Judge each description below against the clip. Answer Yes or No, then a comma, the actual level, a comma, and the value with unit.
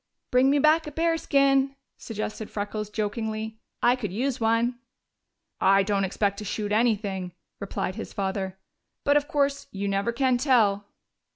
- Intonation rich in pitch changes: No, average, 5.0 semitones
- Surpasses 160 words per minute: No, average, 150 wpm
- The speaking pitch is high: Yes, high, 220 Hz